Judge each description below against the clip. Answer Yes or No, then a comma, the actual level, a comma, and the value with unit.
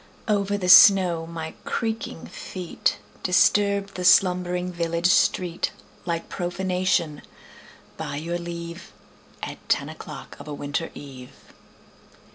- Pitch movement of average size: No, narrow, 1.9 semitones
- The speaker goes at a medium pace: No, slow, 110 wpm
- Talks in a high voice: No, medium, 175 Hz